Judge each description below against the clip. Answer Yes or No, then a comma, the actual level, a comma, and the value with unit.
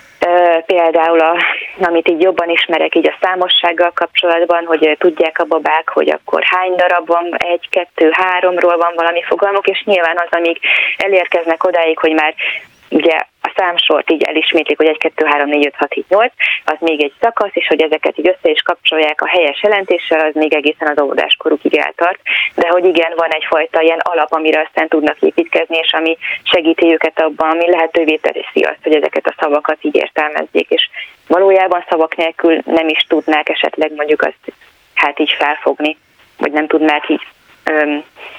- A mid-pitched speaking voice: Yes, medium, 165 Hz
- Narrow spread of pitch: Yes, narrow, 2.0 semitones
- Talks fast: Yes, fast, 175 wpm